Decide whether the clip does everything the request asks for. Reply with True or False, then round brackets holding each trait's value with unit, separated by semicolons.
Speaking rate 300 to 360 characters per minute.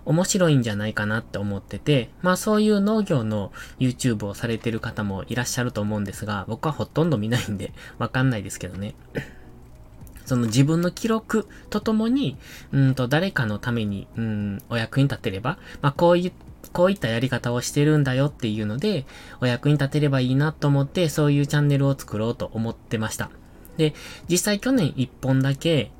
False (395 characters per minute)